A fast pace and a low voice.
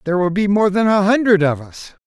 No: fast, 260 wpm; high, 195 Hz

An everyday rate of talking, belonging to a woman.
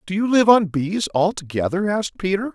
No: average, 190 wpm; male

